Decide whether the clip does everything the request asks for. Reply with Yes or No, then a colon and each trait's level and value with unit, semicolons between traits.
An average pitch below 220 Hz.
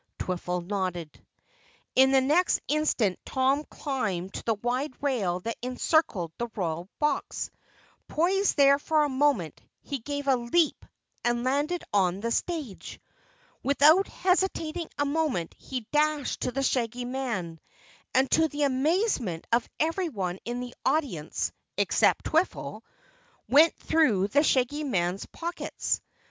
No: very high, 265 Hz